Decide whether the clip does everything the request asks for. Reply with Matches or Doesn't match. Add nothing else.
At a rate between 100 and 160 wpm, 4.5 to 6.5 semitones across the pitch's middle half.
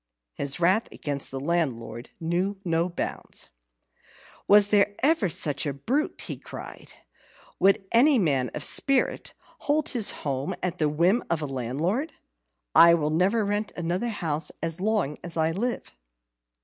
Matches